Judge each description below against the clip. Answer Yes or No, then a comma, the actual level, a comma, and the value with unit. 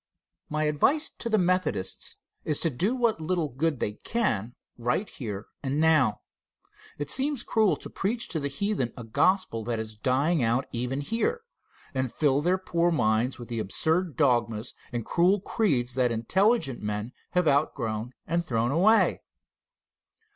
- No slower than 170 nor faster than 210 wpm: No, average, 155 wpm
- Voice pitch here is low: No, medium, 145 Hz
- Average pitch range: No, wide, 7.4 semitones